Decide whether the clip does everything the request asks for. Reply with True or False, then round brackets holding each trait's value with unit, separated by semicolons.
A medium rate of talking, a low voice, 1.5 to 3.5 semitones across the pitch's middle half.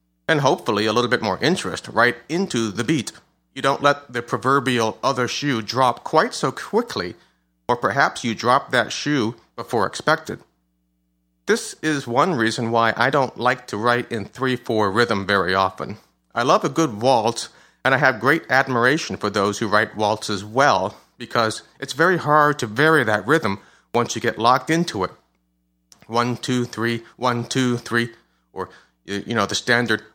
False (175 wpm; 120 Hz; 4.2 semitones)